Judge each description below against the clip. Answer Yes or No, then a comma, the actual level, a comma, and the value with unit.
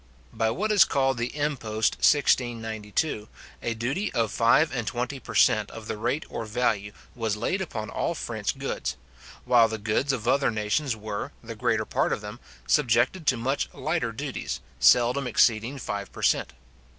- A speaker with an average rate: Yes, average, 170 wpm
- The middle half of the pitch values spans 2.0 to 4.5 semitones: Yes, average, 3.9 semitones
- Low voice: Yes, low, 120 Hz